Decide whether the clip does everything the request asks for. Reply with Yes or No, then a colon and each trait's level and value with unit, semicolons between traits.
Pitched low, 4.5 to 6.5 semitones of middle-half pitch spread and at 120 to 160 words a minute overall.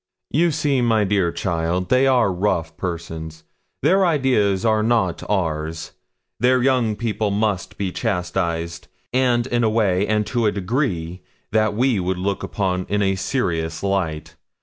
Yes: low, 100 Hz; average, 5.1 semitones; average, 150 wpm